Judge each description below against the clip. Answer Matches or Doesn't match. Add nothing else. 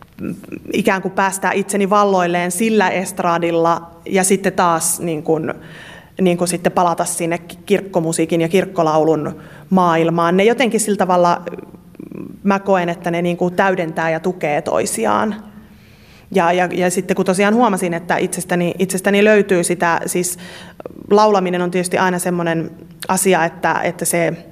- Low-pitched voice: Doesn't match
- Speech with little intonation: Matches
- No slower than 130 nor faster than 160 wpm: Matches